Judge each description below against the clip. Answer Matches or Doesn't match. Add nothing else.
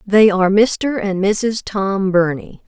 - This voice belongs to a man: Doesn't match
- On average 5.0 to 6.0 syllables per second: Doesn't match